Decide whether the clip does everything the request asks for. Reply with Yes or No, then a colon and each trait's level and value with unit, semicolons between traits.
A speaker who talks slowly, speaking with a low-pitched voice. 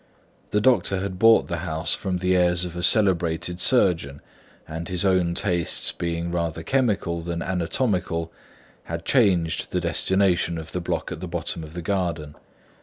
No: average, 165 wpm; very low, 90 Hz